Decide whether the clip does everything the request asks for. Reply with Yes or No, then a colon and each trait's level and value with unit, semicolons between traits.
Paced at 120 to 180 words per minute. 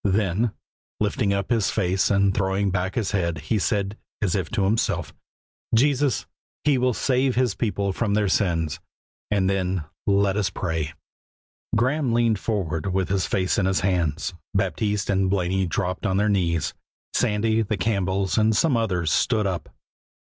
Yes: average, 160 wpm